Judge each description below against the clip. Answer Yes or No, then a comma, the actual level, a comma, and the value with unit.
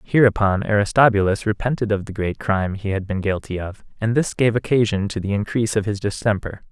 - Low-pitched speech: Yes, low, 105 Hz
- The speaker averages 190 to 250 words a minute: Yes, average, 195 wpm